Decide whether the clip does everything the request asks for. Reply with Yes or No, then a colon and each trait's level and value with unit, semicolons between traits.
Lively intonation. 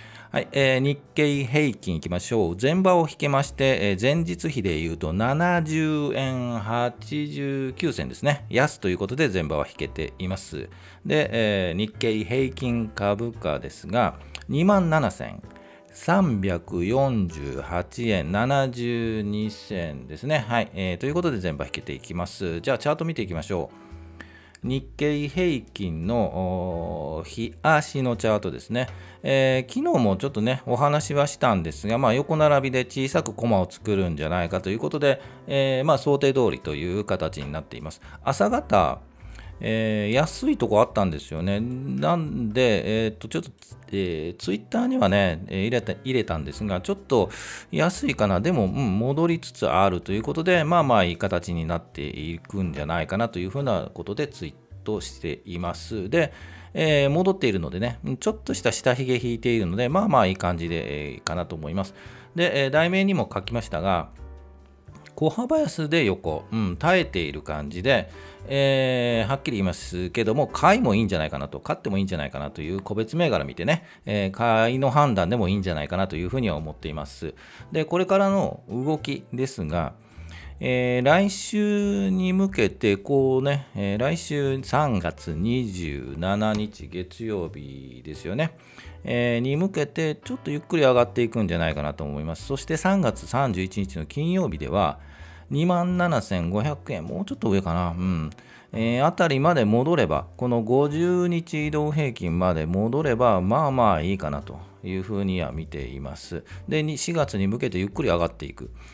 Yes: wide, 8.0 semitones